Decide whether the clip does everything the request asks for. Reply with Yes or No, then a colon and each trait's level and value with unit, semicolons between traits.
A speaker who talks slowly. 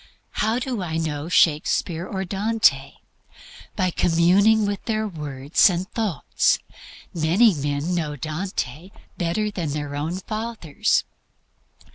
Yes: slow, 115 wpm